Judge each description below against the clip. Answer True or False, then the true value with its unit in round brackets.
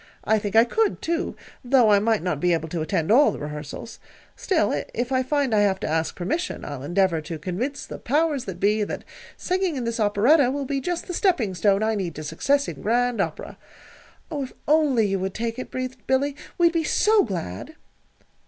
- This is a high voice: True (230 Hz)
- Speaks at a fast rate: True (210 wpm)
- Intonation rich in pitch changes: True (6.9 semitones)